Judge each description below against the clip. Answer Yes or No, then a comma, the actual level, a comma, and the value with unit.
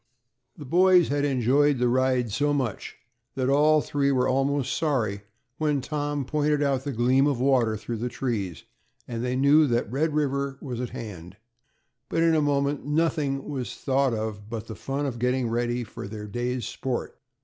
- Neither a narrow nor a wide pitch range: Yes, average, 3.3 semitones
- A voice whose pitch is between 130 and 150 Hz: Yes, low, 135 Hz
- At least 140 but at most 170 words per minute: No, average, 180 wpm